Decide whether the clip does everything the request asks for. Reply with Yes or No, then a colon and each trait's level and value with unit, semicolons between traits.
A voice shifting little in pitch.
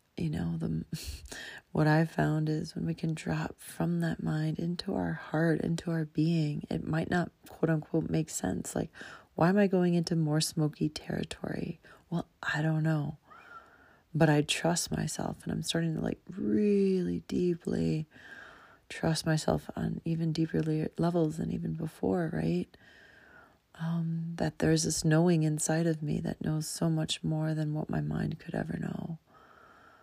Yes: narrow, 1.7 semitones